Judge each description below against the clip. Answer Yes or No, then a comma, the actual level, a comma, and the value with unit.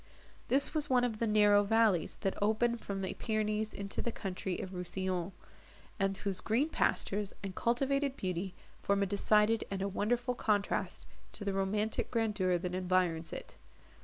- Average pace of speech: Yes, average, 160 wpm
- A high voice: Yes, high, 205 Hz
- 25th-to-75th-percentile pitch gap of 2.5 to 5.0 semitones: Yes, average, 3.0 semitones